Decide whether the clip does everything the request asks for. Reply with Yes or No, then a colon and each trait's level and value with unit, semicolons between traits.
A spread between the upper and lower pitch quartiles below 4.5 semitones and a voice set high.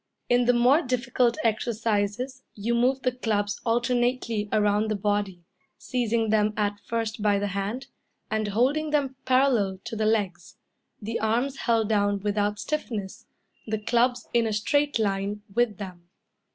Yes: average, 3.1 semitones; high, 220 Hz